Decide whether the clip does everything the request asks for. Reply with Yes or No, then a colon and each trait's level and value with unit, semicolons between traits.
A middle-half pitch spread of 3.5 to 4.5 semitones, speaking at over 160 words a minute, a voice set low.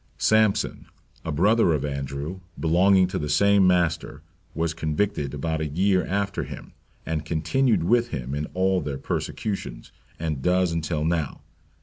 No: average, 4.2 semitones; average, 145 wpm; very low, 85 Hz